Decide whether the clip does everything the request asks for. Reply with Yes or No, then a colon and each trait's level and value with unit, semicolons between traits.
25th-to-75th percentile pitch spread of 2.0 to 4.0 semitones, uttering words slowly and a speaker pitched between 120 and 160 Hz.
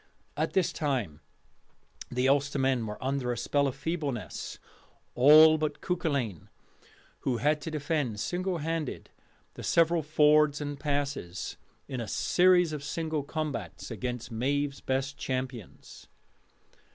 Yes: average, 3.4 semitones; slow, 125 wpm; medium, 140 Hz